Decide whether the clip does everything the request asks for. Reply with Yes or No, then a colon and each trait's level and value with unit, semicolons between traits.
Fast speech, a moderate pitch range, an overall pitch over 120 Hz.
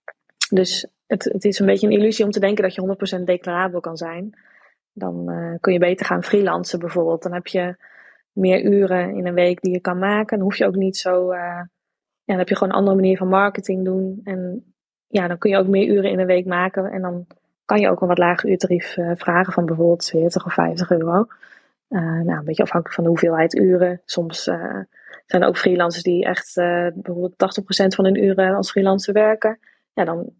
No: fast, 220 wpm; narrow, 1.9 semitones; medium, 185 Hz